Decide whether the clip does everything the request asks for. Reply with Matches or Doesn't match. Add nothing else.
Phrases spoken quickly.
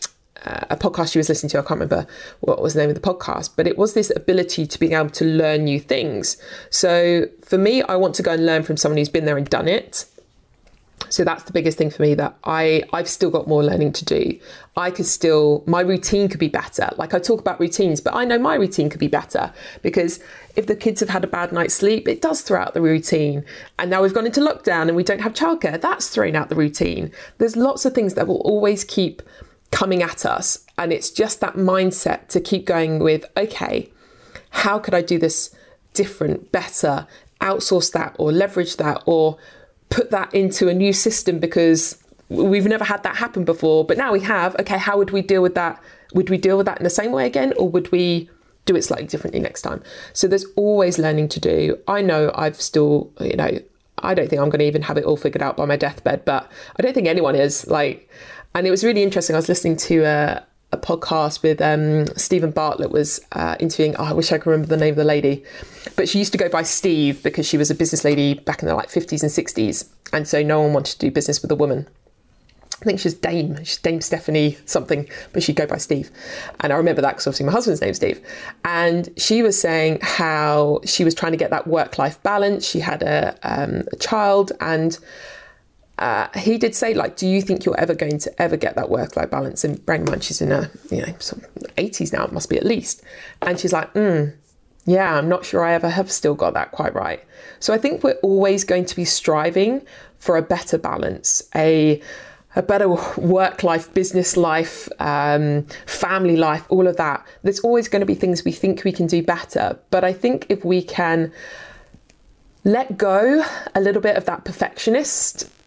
Matches